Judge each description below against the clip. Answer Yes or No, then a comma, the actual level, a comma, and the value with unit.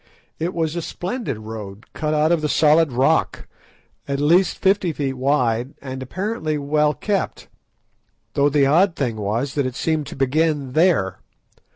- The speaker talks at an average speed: Yes, average, 160 wpm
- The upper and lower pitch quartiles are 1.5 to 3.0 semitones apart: No, average, 3.8 semitones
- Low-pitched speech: No, medium, 150 Hz